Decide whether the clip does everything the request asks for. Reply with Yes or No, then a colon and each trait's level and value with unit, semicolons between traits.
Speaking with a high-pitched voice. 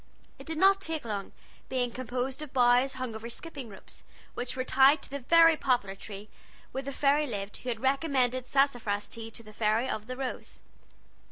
Yes: very high, 255 Hz